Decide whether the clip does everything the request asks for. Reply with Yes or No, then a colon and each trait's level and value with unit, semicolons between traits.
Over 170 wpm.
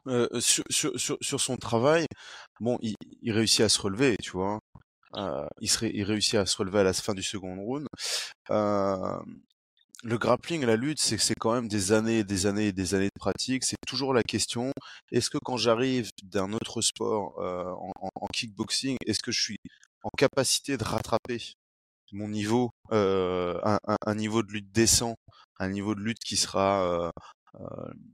Yes: average, 190 wpm